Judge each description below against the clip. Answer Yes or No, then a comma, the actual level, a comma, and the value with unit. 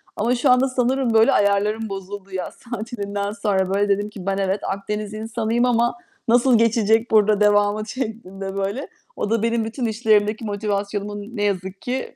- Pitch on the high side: Yes, high, 210 Hz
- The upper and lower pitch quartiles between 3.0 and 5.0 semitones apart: No, narrow, 2.4 semitones